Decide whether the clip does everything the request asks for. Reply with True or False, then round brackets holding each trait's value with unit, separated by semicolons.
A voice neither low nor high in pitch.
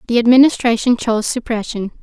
False (235 Hz)